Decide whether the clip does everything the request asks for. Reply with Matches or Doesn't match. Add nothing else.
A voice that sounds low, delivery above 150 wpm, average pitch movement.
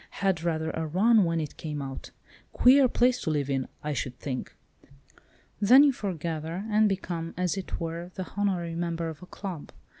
Doesn't match